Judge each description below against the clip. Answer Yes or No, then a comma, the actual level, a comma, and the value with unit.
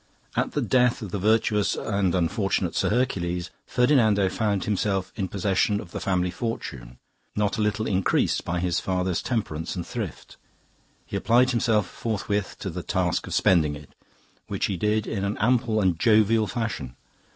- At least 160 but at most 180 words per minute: Yes, average, 165 wpm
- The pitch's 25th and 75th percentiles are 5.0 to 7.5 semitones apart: No, average, 3.5 semitones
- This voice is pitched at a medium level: No, low, 100 Hz